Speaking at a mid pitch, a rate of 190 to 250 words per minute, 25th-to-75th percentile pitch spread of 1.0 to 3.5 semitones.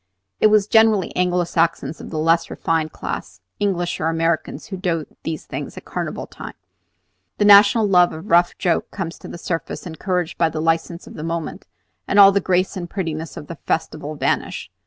Yes: medium, 170 Hz; average, 195 wpm; average, 2.7 semitones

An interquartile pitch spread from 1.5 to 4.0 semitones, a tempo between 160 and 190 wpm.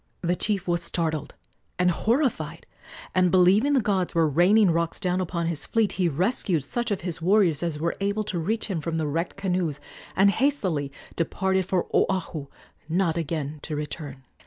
Yes: average, 3.4 semitones; average, 175 wpm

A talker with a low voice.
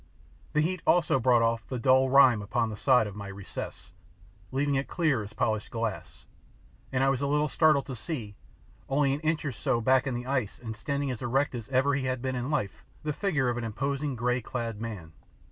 Yes: low, 130 Hz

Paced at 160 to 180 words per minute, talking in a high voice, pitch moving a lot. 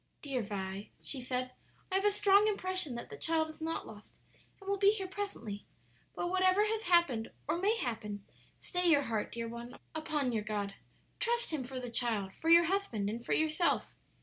No: average, 195 wpm; very high, 310 Hz; wide, 8.4 semitones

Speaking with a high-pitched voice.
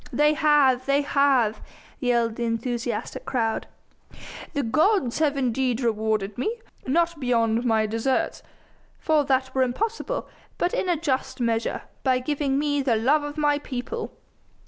Yes: very high, 260 Hz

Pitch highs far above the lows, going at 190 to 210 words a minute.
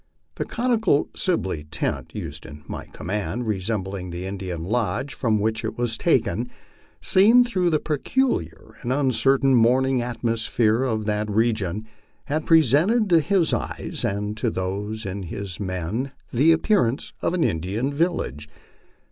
No: wide, 6.6 semitones; average, 140 wpm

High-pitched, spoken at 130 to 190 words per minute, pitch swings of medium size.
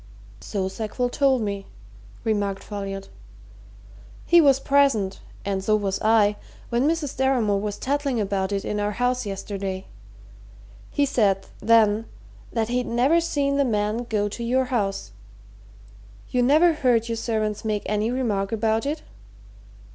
Yes: high, 220 Hz; average, 140 wpm; average, 4.0 semitones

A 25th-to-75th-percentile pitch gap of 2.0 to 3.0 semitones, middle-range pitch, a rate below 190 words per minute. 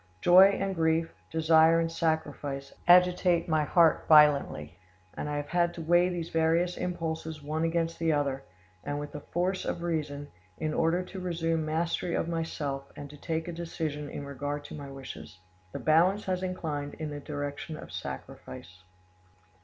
Yes: average, 2.7 semitones; medium, 160 Hz; average, 170 wpm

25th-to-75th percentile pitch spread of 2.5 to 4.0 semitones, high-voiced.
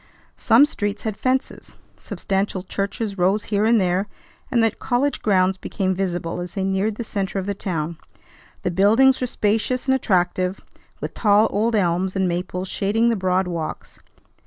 Yes: average, 3.1 semitones; high, 195 Hz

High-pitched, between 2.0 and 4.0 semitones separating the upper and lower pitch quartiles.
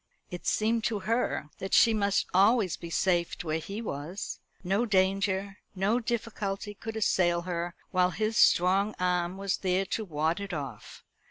Yes: high, 195 Hz; average, 3.1 semitones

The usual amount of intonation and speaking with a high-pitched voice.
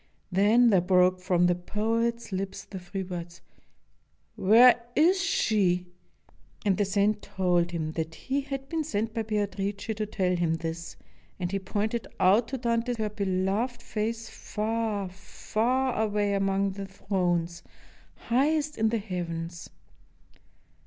Yes: average, 3.9 semitones; high, 200 Hz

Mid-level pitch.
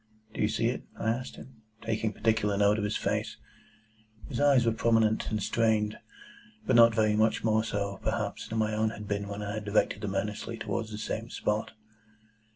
No: low, 110 Hz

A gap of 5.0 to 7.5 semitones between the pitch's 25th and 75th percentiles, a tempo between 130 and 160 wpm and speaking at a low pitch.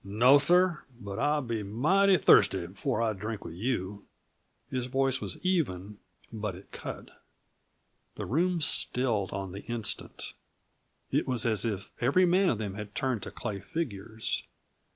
Yes: wide, 5.6 semitones; average, 150 wpm; low, 115 Hz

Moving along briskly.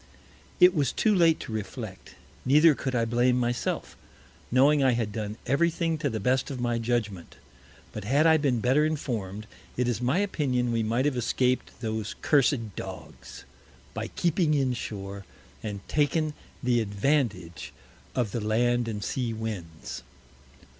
No: average, 155 wpm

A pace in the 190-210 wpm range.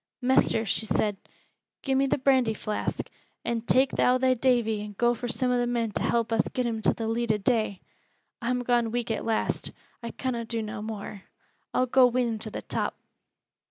Yes: fast, 205 wpm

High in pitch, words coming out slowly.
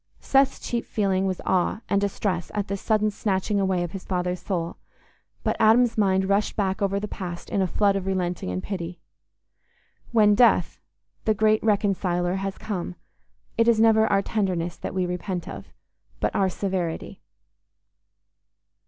No: high, 195 Hz; average, 160 wpm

